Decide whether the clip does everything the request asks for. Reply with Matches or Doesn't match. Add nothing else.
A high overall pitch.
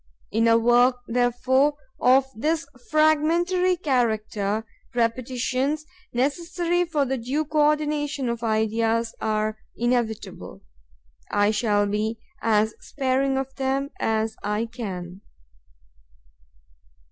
Matches